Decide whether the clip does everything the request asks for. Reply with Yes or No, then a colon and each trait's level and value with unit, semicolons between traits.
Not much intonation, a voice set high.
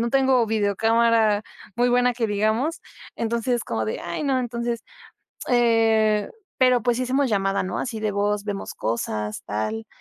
No: average, 3.1 semitones; high, 225 Hz